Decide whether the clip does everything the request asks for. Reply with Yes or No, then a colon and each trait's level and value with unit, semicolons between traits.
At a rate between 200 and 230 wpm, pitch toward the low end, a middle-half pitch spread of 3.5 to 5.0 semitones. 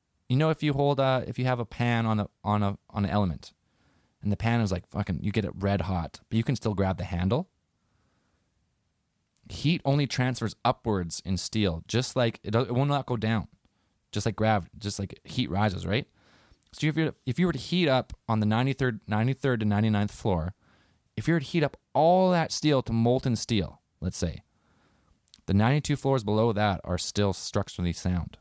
Yes: fast, 205 wpm; low, 110 Hz; average, 4.7 semitones